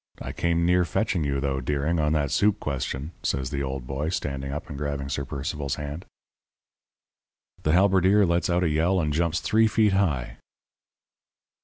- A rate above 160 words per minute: Yes, average, 170 wpm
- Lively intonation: No, average, 4.2 semitones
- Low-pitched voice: Yes, very low, 75 Hz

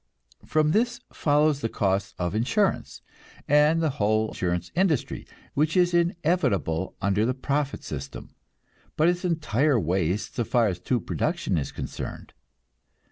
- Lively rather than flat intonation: Yes, wide, 8.1 semitones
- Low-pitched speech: Yes, low, 130 Hz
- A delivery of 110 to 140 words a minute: Yes, slow, 135 wpm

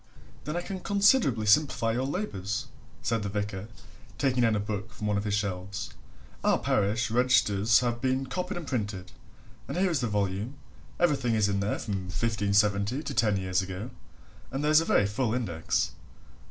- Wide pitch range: No, average, 4.7 semitones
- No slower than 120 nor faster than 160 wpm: No, average, 180 wpm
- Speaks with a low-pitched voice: Yes, low, 110 Hz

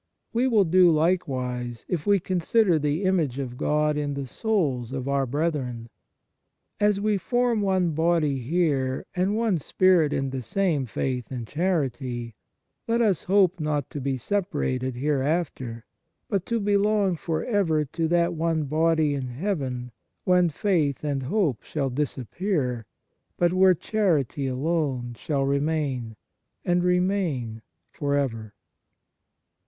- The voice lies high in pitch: No, medium, 155 Hz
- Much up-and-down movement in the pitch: Yes, wide, 5.7 semitones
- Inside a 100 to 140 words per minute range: Yes, slow, 135 wpm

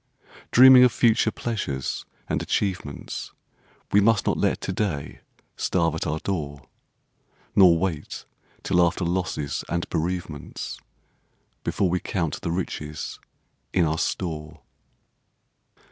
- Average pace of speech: No, slow, 115 wpm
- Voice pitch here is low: Yes, very low, 85 Hz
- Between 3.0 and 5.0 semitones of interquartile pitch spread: Yes, average, 4.0 semitones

